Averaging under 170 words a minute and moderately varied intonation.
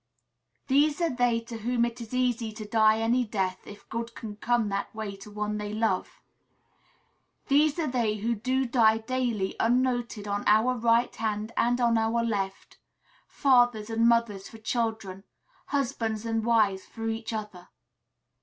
No: average, 160 wpm; narrow, 2.3 semitones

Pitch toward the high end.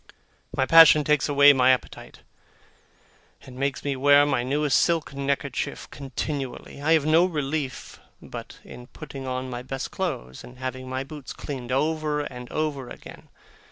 No: medium, 140 Hz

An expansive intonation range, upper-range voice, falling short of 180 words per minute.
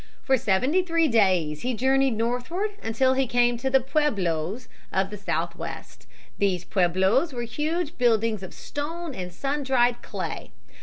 Yes: wide, 5.8 semitones; high, 240 Hz; average, 160 wpm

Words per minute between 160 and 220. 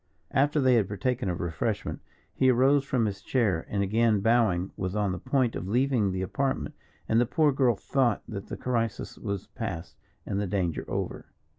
Yes: average, 185 wpm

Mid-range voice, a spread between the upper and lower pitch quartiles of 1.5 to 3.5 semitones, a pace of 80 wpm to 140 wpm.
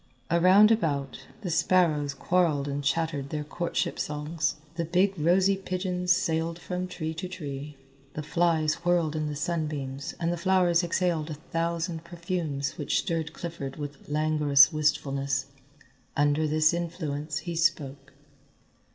Yes: medium, 160 Hz; average, 2.9 semitones; slow, 135 wpm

